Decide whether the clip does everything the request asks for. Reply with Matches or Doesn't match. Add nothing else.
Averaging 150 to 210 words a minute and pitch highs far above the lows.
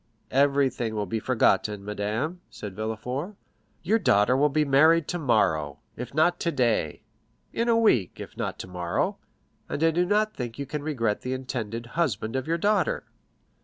Matches